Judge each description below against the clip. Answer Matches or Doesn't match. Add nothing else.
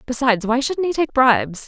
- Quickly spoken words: Matches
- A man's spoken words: Doesn't match